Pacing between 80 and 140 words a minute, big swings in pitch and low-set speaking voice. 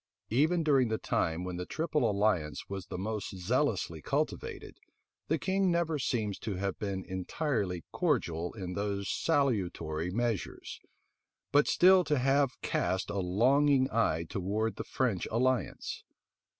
Yes: slow, 135 wpm; wide, 7.1 semitones; low, 110 Hz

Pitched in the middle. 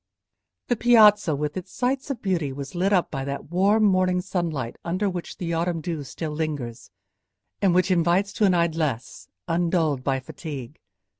Yes: medium, 170 Hz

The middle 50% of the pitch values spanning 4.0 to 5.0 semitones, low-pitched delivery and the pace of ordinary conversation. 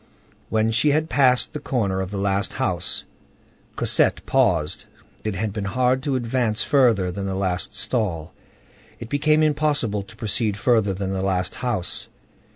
Yes: average, 4.7 semitones; low, 110 Hz; average, 160 wpm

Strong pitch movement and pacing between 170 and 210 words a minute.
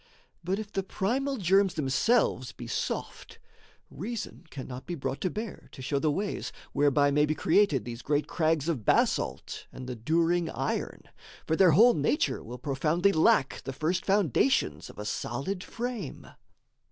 No: wide, 6.2 semitones; average, 160 wpm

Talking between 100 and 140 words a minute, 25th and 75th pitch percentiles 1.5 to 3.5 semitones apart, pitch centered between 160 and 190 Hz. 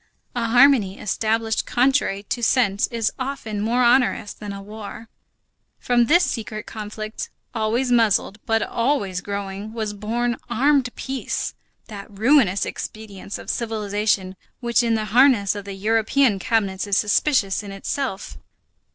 No: slow, 135 wpm; average, 3.0 semitones; high, 220 Hz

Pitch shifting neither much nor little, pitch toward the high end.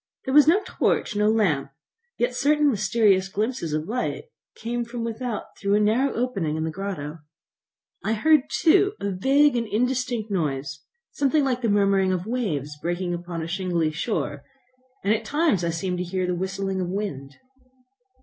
No: wide, 5.8 semitones; high, 200 Hz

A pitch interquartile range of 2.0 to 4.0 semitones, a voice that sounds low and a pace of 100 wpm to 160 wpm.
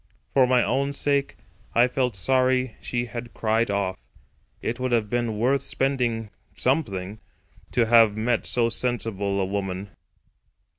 Yes: average, 3.5 semitones; low, 120 Hz; slow, 135 wpm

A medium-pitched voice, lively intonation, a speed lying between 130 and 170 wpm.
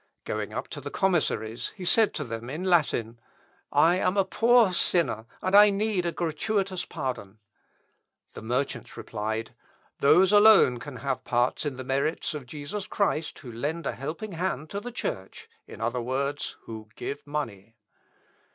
Yes: medium, 150 Hz; wide, 7.4 semitones; average, 160 wpm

